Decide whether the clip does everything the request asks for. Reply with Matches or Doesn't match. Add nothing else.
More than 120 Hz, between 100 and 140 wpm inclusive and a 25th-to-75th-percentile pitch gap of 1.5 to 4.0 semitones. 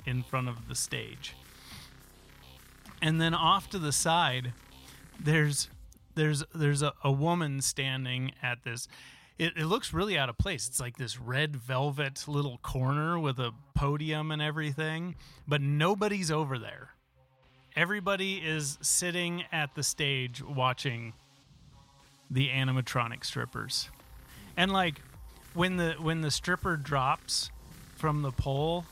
Matches